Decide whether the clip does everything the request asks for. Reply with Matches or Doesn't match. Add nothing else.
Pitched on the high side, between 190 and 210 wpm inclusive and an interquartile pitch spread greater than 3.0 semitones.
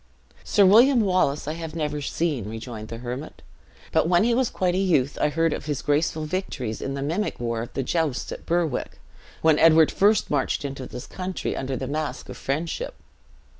Doesn't match